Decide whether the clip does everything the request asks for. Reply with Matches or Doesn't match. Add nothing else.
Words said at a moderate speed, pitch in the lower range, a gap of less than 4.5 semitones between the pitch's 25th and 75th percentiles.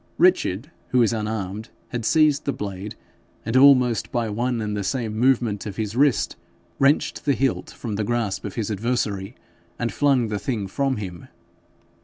Matches